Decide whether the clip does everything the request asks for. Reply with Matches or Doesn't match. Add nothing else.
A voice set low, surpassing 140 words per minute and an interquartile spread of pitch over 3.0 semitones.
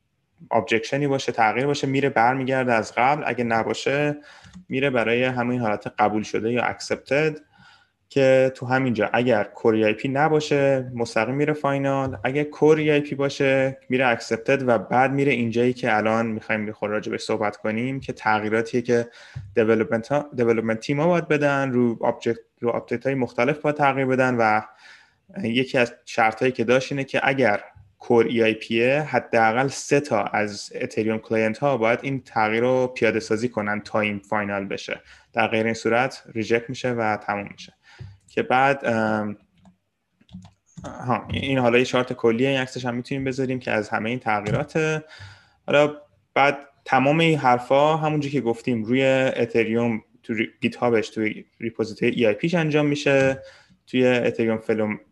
Matches